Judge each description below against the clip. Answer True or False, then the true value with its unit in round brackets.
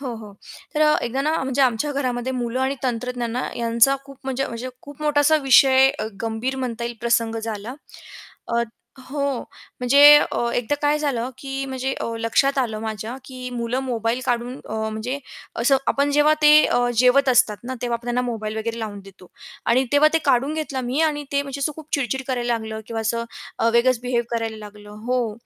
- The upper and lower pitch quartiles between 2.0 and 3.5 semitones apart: True (2.8 semitones)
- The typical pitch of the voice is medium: False (250 Hz)